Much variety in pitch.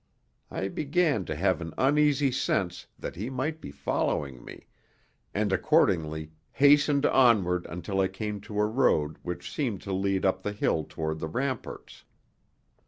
Yes: wide, 7.5 semitones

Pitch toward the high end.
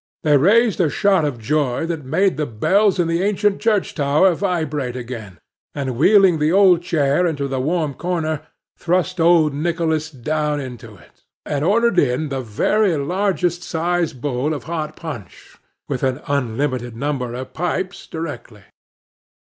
No: medium, 155 Hz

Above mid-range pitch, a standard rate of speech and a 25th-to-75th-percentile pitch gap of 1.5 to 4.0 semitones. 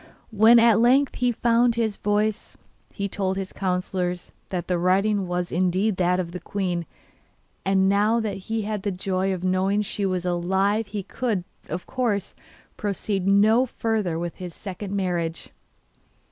Yes: high, 195 Hz; average, 160 wpm; average, 2.9 semitones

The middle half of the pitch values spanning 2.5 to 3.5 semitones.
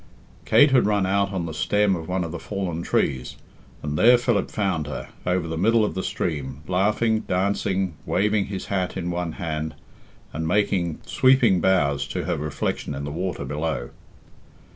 No: average, 4.1 semitones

